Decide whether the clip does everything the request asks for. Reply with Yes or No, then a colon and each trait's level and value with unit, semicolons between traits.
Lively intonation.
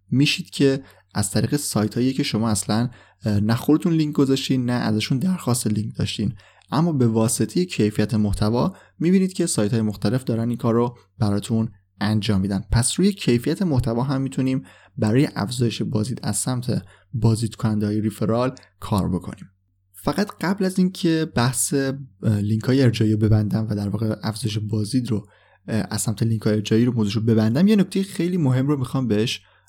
No: average, 4.1 semitones